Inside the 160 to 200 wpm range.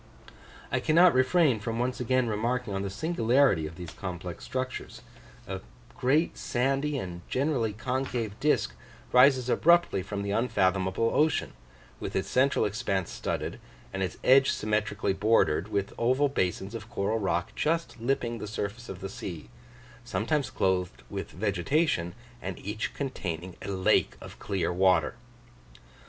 No: average, 145 wpm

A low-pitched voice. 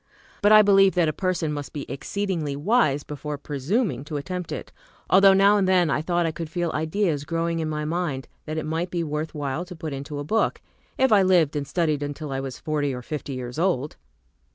No: medium, 160 Hz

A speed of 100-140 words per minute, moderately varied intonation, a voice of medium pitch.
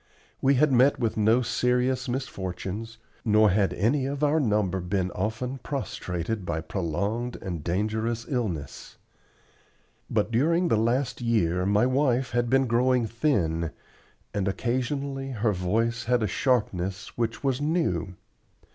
No: slow, 135 wpm; average, 4.8 semitones; low, 115 Hz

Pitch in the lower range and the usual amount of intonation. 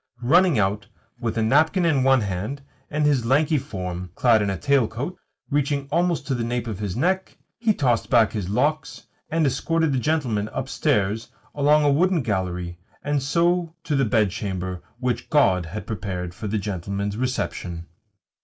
No: low, 120 Hz; wide, 6.6 semitones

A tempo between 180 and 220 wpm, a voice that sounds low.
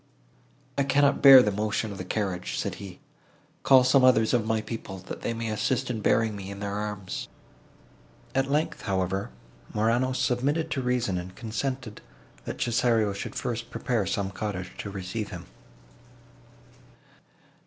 No: average, 155 wpm; low, 110 Hz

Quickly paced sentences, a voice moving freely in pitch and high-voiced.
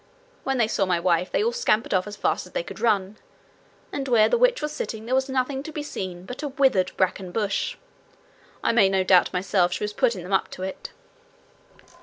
Yes: fast, 220 wpm; wide, 6.2 semitones; high, 215 Hz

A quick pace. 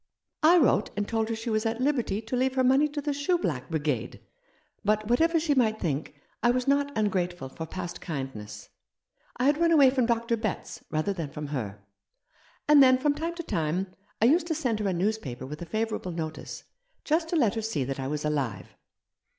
Yes: fast, 215 wpm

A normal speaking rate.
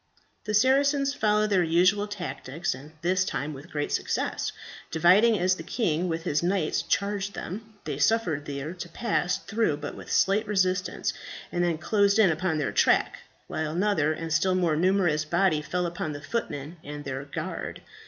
Yes: average, 175 wpm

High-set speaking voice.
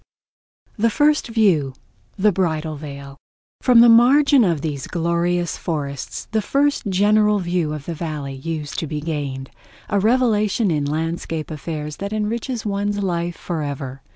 No: medium, 170 Hz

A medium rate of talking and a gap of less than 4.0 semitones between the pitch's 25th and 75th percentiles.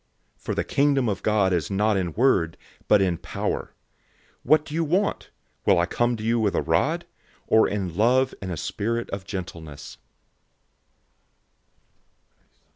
No: average, 160 wpm; average, 4.7 semitones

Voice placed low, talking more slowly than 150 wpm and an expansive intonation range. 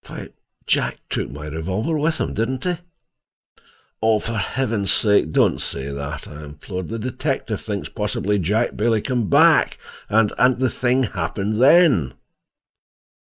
Yes: low, 110 Hz; average, 140 wpm; wide, 6.8 semitones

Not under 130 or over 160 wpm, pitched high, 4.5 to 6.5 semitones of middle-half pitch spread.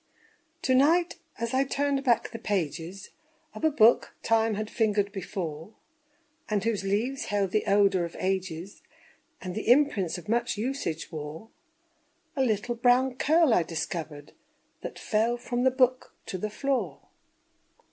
Yes: average, 145 wpm; high, 215 Hz; average, 5.1 semitones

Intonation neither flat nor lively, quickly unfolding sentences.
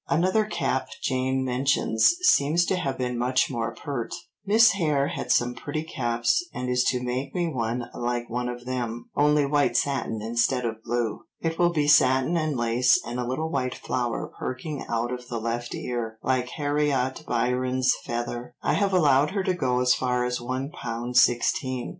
No: average, 3.2 semitones; average, 180 wpm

